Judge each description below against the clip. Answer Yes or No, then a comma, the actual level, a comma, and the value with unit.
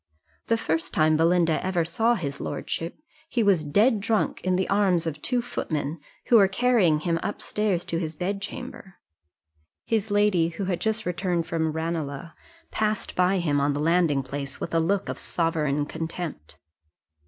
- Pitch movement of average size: Yes, average, 4.1 semitones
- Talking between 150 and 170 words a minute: Yes, average, 165 wpm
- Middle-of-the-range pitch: Yes, medium, 175 Hz